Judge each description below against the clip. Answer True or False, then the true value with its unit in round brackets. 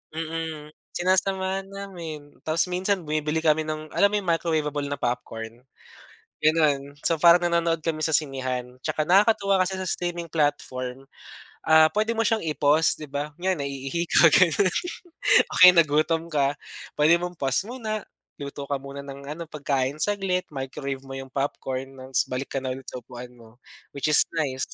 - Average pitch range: True (3.9 semitones)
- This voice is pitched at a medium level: True (155 Hz)